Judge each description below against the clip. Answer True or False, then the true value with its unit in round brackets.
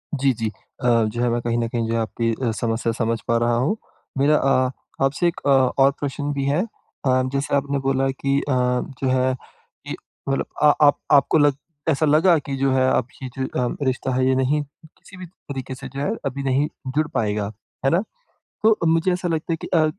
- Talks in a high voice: False (135 Hz)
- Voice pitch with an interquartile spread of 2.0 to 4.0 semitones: True (2.7 semitones)